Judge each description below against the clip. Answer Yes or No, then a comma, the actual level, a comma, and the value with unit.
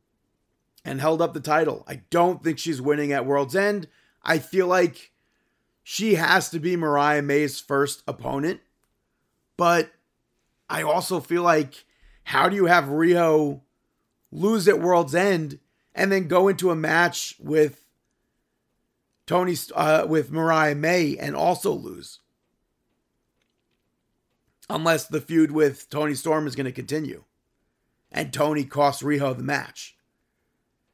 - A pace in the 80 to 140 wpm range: Yes, slow, 135 wpm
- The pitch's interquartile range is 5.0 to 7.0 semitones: No, average, 2.9 semitones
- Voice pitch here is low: No, medium, 160 Hz